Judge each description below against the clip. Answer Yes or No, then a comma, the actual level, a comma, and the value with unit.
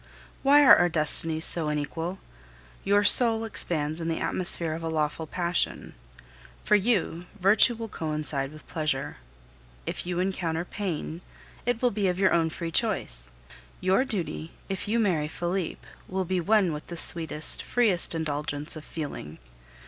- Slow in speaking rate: No, average, 155 wpm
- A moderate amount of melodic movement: Yes, average, 3.7 semitones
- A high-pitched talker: No, medium, 170 Hz